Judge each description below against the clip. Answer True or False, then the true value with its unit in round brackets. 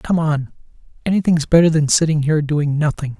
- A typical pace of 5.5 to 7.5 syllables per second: True (5.8 syllables/s)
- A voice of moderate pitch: True (155 Hz)